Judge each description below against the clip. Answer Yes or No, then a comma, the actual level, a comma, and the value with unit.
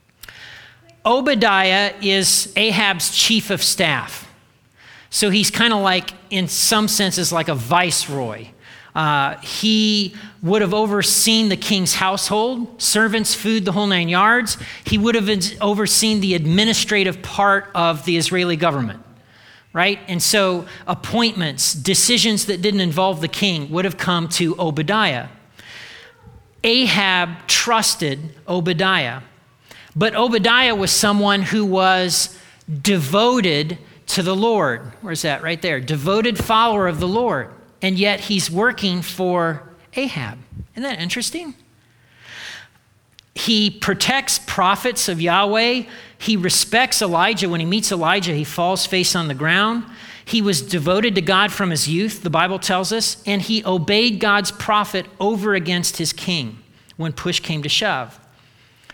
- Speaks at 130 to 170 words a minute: Yes, slow, 135 wpm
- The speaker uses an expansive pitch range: No, average, 3.8 semitones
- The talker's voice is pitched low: No, high, 190 Hz